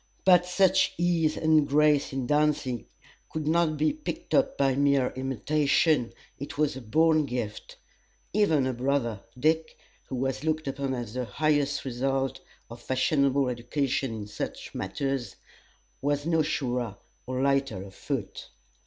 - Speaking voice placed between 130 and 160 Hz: Yes, medium, 140 Hz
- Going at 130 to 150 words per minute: Yes, average, 145 wpm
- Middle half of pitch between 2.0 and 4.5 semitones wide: Yes, average, 3.3 semitones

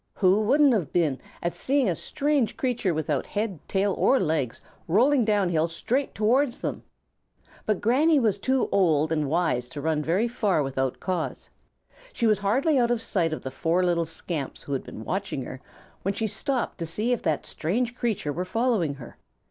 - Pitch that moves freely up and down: Yes, wide, 6.9 semitones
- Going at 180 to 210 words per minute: Yes, average, 190 wpm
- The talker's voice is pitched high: Yes, high, 195 Hz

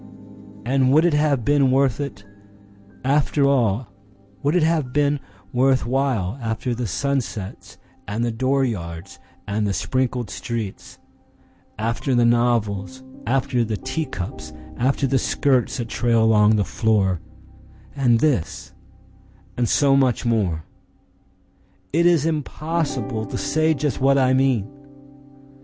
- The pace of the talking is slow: Yes, slow, 115 wpm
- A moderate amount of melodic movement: Yes, average, 4.3 semitones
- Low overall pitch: Yes, low, 125 Hz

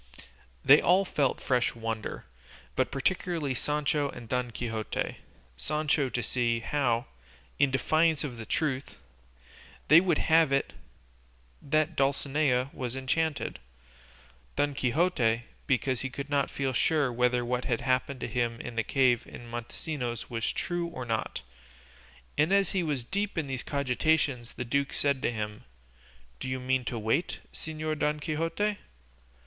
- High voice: No, low, 135 Hz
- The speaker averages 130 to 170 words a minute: Yes, average, 145 wpm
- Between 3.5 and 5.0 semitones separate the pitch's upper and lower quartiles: Yes, average, 4.1 semitones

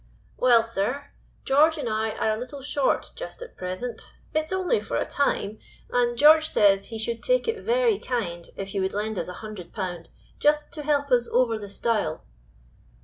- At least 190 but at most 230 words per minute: Yes, average, 195 wpm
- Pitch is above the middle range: Yes, high, 240 Hz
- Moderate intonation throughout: No, wide, 6.2 semitones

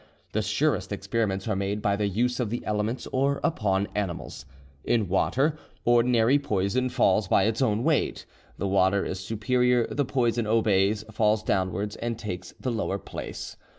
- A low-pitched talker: Yes, low, 110 Hz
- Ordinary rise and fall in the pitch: Yes, average, 3.5 semitones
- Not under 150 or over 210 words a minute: Yes, average, 160 wpm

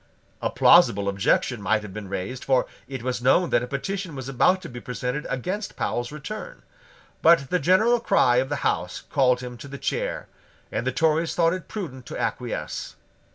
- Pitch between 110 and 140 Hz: Yes, low, 135 Hz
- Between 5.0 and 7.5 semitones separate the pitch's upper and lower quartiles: Yes, wide, 5.5 semitones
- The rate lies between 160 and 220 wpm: Yes, average, 190 wpm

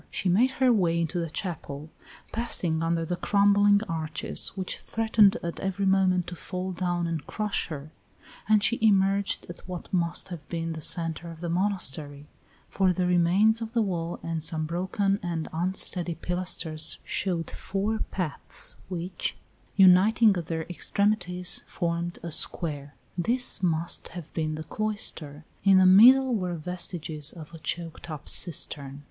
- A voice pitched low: No, medium, 175 Hz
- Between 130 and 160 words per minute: Yes, average, 155 wpm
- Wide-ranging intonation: No, average, 3.1 semitones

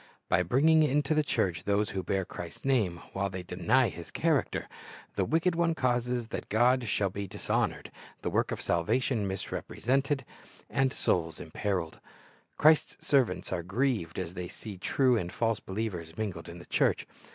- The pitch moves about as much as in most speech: No, wide, 6.7 semitones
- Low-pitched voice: Yes, low, 105 Hz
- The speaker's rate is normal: Yes, average, 165 wpm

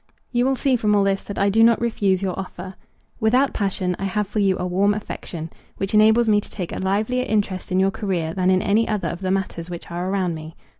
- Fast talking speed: Yes, fast, 245 wpm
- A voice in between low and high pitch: No, high, 195 Hz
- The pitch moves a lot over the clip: No, narrow, 2.6 semitones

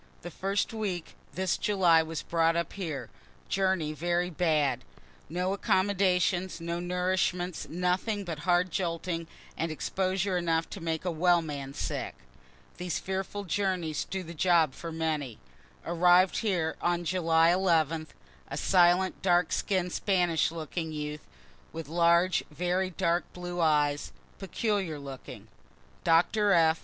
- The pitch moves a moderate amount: No, narrow, 2.3 semitones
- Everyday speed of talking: No, slow, 130 wpm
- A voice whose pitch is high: No, medium, 175 Hz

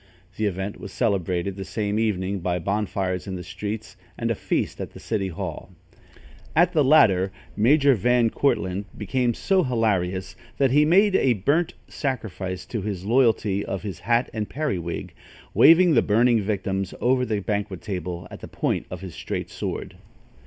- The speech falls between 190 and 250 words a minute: No, average, 165 wpm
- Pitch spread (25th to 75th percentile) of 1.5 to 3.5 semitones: No, average, 4.7 semitones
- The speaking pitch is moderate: No, low, 105 Hz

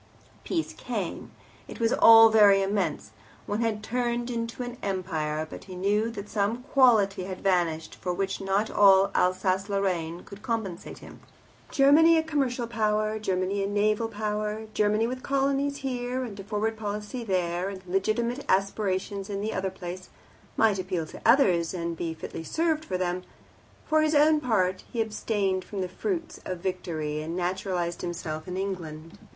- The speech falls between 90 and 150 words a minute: No, average, 165 wpm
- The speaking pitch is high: Yes, high, 200 Hz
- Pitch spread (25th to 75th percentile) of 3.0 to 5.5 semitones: Yes, average, 3.9 semitones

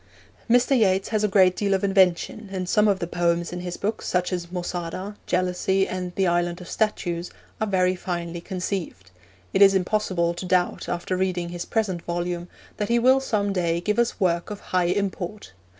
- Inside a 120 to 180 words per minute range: No, average, 190 wpm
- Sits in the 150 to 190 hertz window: Yes, medium, 185 Hz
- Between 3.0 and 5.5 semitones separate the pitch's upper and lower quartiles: No, narrow, 2.5 semitones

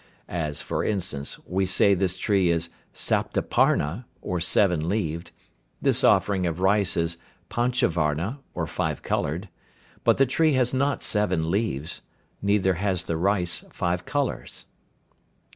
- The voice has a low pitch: Yes, very low, 95 Hz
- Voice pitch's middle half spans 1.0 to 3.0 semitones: No, average, 3.7 semitones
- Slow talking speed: Yes, slow, 130 wpm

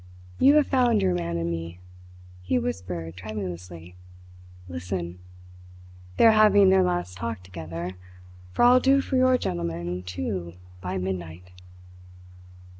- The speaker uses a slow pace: Yes, slow, 125 wpm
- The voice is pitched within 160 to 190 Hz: No, very low, 90 Hz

